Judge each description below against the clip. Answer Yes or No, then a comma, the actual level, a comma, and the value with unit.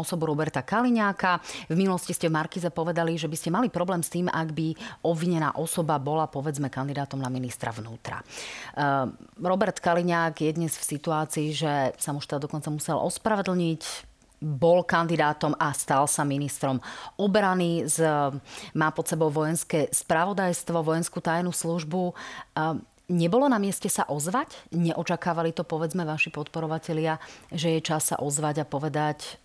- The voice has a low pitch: No, medium, 165 Hz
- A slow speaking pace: No, average, 145 wpm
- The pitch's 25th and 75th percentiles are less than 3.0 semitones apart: Yes, narrow, 2.5 semitones